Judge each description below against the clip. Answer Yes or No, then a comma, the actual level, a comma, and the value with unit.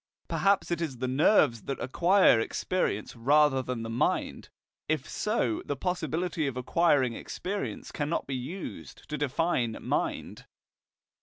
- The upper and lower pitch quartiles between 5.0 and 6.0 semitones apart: Yes, average, 5.3 semitones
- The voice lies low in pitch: No, medium, 145 Hz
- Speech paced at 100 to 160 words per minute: Yes, slow, 135 wpm